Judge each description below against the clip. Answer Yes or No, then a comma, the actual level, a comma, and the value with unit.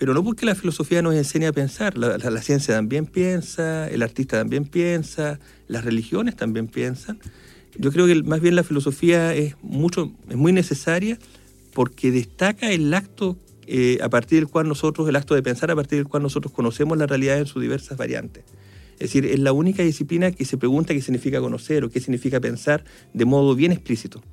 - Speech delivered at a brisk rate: Yes, fast, 195 wpm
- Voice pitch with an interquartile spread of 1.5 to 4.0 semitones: No, average, 4.6 semitones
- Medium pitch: Yes, medium, 145 Hz